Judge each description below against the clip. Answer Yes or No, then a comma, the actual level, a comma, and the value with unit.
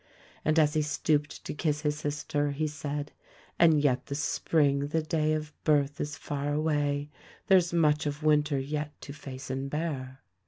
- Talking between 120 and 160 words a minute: No, average, 180 wpm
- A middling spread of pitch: No, narrow, 1.3 semitones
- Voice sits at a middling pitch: Yes, medium, 150 Hz